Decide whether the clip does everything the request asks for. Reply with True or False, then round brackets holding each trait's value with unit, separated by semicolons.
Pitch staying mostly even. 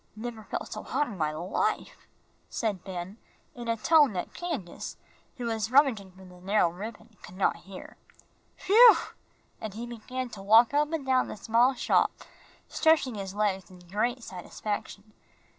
False (4.8 semitones)